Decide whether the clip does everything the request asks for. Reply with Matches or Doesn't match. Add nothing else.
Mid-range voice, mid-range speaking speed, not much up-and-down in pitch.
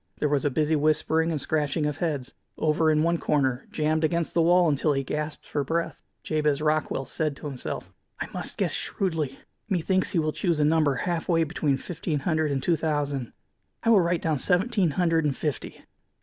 Matches